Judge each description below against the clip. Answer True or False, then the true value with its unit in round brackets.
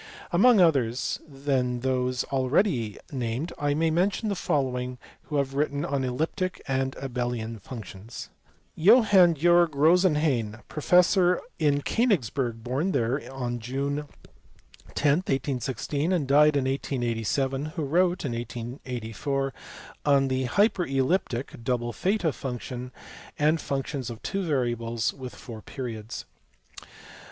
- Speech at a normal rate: False (115 wpm)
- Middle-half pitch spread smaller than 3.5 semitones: False (4.3 semitones)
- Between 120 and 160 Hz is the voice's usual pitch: True (135 Hz)